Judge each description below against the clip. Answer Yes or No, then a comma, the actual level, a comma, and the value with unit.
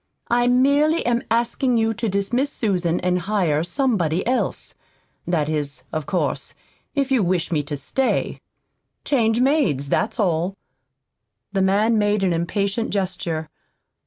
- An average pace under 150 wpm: Yes, slow, 135 wpm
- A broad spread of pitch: Yes, wide, 5.9 semitones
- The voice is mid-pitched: No, high, 200 Hz